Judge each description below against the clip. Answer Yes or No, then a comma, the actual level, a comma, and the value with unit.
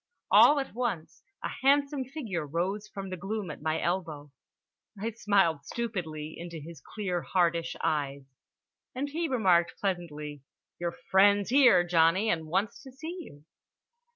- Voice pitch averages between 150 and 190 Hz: Yes, medium, 185 Hz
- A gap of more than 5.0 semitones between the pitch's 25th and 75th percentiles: Yes, wide, 5.6 semitones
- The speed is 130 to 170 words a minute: Yes, average, 145 wpm